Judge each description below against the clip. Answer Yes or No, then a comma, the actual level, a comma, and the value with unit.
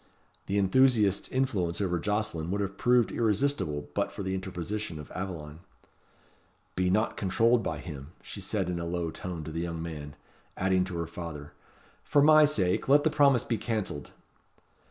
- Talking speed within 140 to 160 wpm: No, average, 170 wpm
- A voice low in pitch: Yes, very low, 95 Hz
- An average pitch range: Yes, average, 4.8 semitones